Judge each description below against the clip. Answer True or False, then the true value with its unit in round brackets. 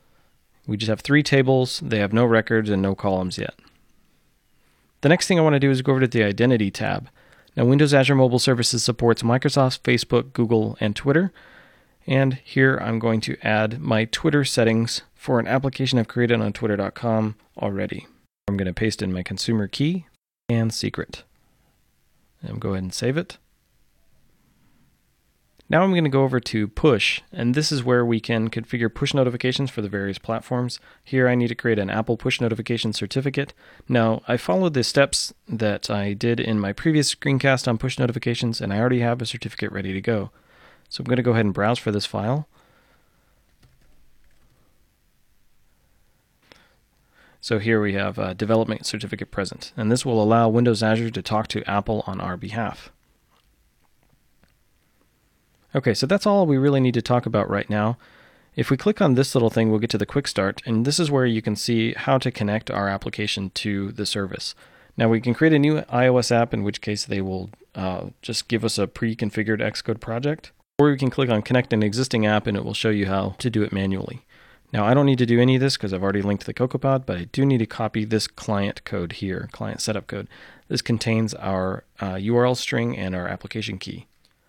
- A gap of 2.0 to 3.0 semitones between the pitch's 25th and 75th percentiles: False (3.5 semitones)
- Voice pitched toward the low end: True (115 Hz)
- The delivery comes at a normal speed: True (195 wpm)